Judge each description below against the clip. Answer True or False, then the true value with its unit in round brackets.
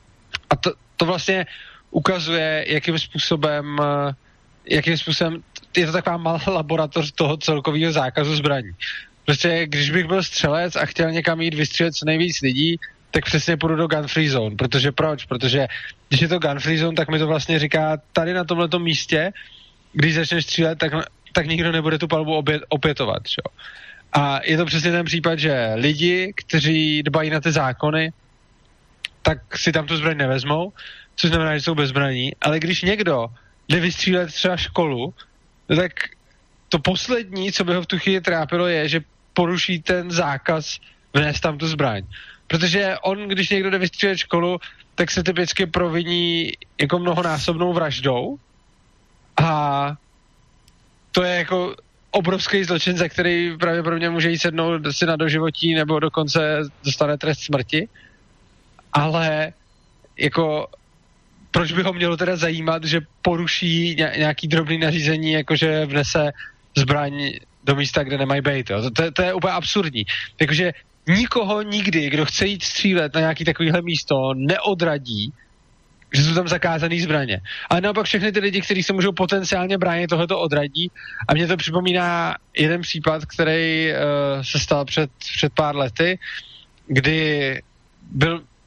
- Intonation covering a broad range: False (2.8 semitones)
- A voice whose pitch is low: False (160 Hz)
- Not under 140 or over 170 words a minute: True (150 wpm)